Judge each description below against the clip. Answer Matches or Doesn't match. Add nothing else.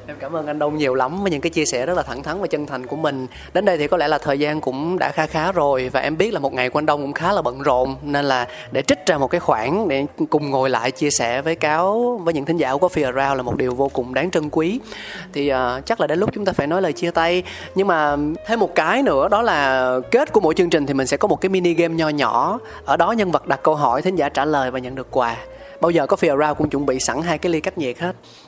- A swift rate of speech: Matches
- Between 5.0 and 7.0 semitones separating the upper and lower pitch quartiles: Doesn't match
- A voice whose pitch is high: Doesn't match